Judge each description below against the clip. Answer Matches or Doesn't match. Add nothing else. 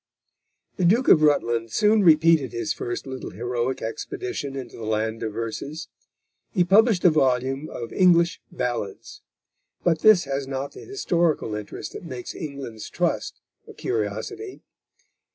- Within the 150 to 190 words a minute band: Doesn't match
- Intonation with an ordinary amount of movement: Doesn't match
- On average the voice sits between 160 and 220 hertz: Doesn't match